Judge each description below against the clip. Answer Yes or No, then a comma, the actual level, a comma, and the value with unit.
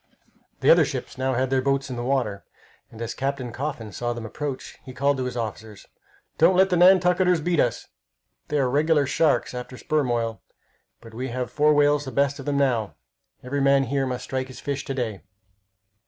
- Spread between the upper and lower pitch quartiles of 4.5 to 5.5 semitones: No, average, 3.0 semitones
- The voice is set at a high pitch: No, low, 135 Hz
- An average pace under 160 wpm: No, average, 200 wpm